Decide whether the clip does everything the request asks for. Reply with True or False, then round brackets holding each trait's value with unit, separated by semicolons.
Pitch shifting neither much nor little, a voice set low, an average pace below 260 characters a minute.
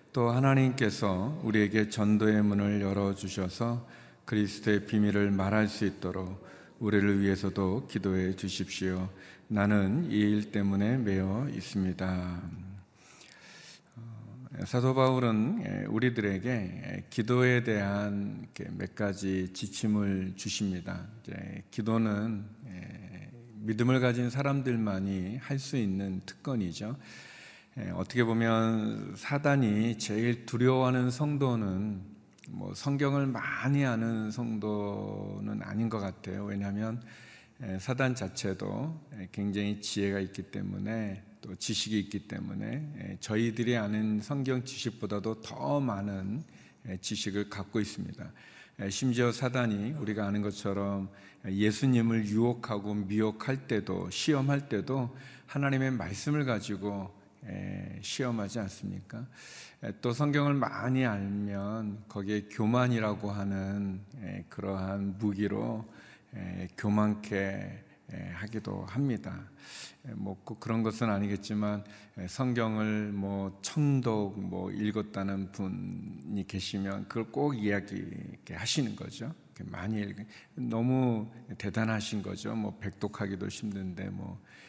True (3.1 semitones; 105 Hz; 245 characters per minute)